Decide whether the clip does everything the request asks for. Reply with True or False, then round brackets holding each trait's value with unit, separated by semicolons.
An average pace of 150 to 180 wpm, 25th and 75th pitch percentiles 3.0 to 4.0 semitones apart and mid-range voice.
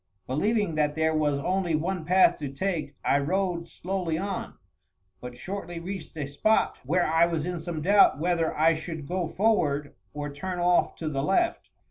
True (175 wpm; 3.7 semitones; 165 Hz)